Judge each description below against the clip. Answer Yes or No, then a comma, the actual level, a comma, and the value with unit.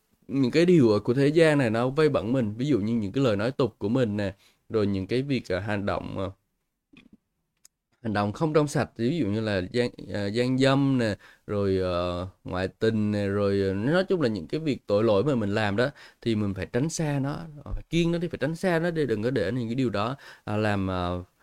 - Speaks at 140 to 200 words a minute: No, average, 245 wpm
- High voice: No, low, 115 Hz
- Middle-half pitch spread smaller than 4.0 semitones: No, average, 5.3 semitones